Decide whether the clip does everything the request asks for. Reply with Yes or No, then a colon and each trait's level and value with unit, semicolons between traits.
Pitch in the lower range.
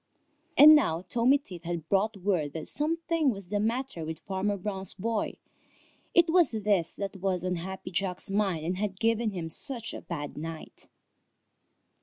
No: high, 195 Hz